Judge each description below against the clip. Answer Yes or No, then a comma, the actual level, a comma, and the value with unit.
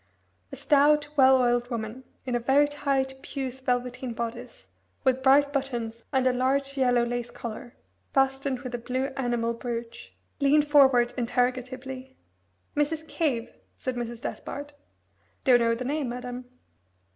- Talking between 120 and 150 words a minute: Yes, average, 140 wpm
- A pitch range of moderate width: No, narrow, 2.2 semitones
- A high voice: Yes, very high, 255 Hz